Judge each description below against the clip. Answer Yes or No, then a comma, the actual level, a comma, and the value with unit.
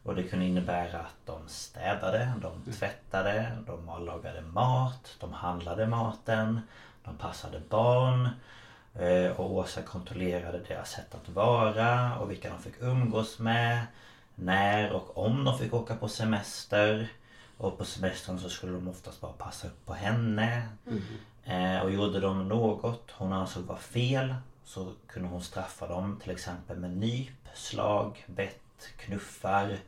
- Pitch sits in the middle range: No, low, 105 Hz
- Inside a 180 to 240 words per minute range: No, average, 145 wpm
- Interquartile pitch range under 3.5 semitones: No, average, 4.1 semitones